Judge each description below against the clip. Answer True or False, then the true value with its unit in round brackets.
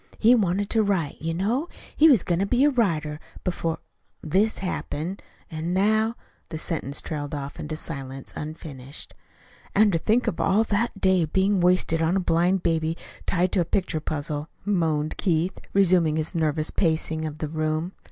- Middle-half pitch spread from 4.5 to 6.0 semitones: False (4.0 semitones)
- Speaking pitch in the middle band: True (170 Hz)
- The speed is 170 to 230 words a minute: True (180 wpm)